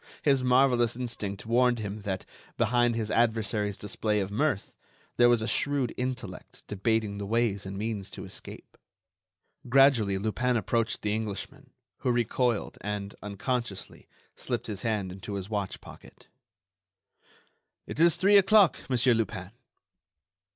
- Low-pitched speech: Yes, low, 110 Hz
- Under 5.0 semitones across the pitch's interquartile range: Yes, average, 3.4 semitones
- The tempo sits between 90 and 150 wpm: Yes, slow, 135 wpm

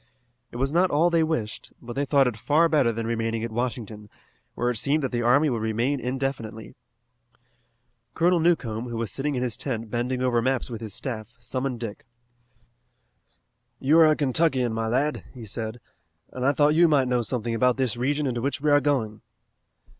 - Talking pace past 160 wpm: Yes, average, 190 wpm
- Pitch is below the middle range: Yes, low, 125 Hz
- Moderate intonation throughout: Yes, average, 3.7 semitones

